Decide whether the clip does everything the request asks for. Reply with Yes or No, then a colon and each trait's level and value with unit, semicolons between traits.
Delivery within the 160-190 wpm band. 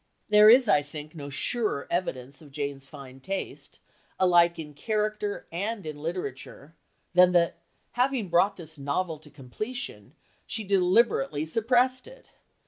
No: slow, 135 wpm